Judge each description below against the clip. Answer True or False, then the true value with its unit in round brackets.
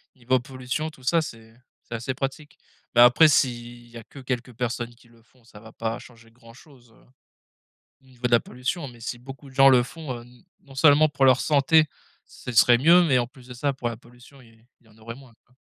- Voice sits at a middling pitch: False (125 Hz)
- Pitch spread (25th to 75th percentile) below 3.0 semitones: True (2.4 semitones)